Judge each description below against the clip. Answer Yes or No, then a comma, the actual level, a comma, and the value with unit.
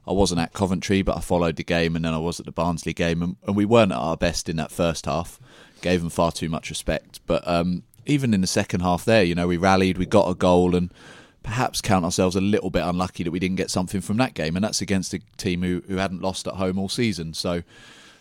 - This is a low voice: Yes, very low, 90 Hz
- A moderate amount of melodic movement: No, narrow, 2.2 semitones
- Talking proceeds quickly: Yes, fast, 265 wpm